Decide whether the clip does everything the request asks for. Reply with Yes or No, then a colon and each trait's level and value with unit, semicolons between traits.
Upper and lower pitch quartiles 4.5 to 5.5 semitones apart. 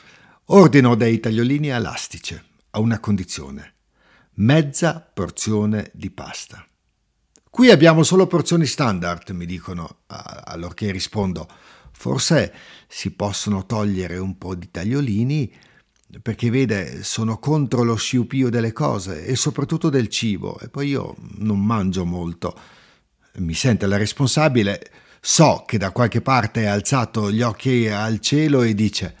Yes: average, 5.0 semitones